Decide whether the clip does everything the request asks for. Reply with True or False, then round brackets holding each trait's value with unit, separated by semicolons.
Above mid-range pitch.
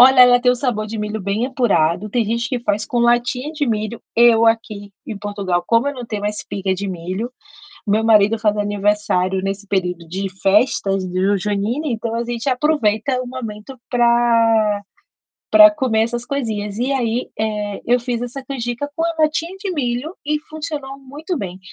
True (230 Hz)